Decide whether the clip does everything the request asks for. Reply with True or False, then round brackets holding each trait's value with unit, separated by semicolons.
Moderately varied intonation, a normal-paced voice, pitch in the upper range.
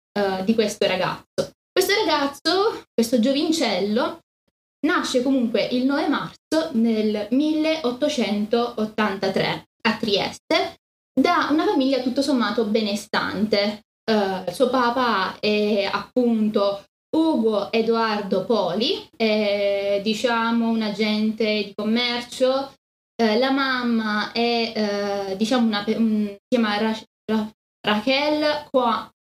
False (4.0 semitones; 100 wpm; 230 Hz)